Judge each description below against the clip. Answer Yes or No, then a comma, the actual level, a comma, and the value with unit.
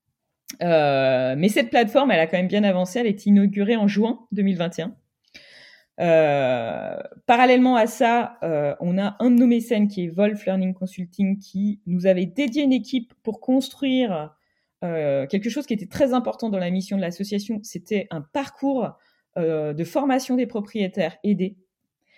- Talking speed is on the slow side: No, average, 165 wpm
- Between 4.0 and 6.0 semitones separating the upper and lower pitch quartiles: Yes, average, 5.1 semitones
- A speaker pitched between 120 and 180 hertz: No, high, 205 Hz